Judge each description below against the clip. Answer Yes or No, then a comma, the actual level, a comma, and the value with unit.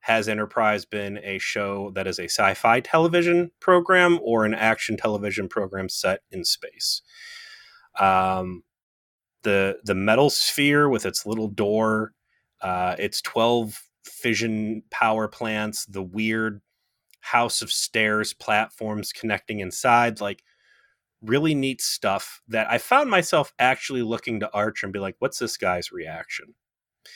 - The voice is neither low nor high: No, low, 110 Hz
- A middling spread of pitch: Yes, average, 3.1 semitones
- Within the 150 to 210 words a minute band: No, slow, 135 wpm